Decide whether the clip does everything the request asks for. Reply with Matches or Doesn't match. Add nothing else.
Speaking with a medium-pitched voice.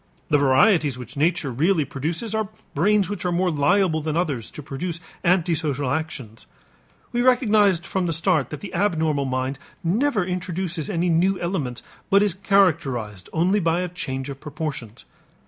Matches